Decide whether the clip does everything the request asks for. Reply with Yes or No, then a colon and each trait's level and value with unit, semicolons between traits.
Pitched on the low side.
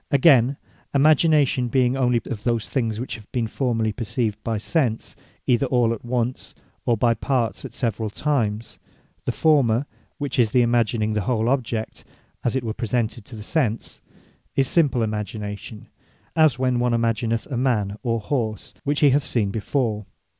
Yes: low, 120 Hz